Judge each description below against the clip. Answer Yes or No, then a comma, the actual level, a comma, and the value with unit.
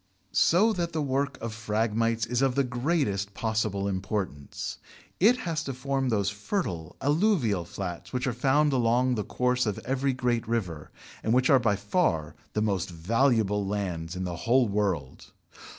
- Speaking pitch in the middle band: No, low, 115 Hz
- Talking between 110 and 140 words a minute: No, average, 165 wpm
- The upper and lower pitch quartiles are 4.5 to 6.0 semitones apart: Yes, average, 5.1 semitones